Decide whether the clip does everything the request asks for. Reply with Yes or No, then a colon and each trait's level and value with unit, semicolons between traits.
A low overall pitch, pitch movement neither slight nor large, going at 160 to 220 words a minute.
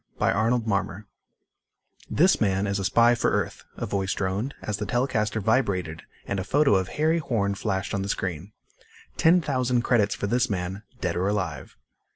Yes: low, 105 Hz; average, 4.1 semitones; average, 180 wpm